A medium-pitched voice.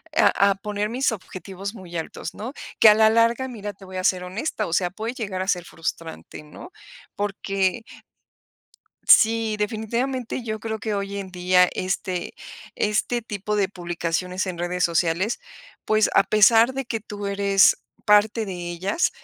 No: high, 200 Hz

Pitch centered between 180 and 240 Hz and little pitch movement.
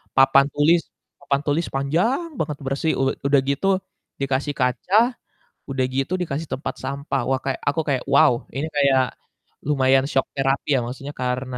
No: medium, 140 Hz; narrow, 1.7 semitones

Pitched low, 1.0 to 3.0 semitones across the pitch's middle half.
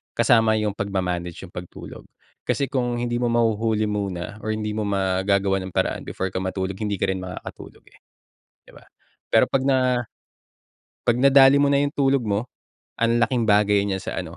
No: low, 105 Hz; average, 3.9 semitones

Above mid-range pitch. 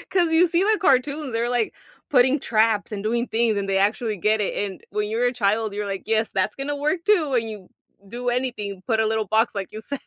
Yes: high, 225 Hz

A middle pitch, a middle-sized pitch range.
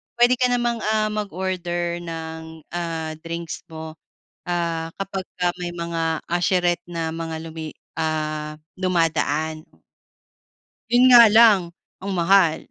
Yes: medium, 170 Hz; average, 3.0 semitones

